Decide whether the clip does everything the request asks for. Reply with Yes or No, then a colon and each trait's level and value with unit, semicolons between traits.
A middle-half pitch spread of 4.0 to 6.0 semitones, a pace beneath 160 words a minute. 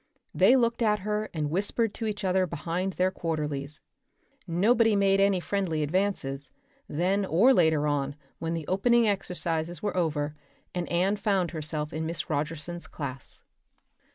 Yes: average, 4.4 semitones; average, 150 wpm